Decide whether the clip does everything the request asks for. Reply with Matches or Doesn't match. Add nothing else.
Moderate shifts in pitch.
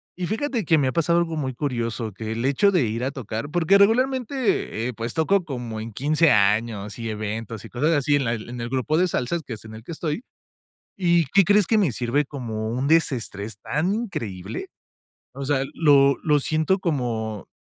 Doesn't match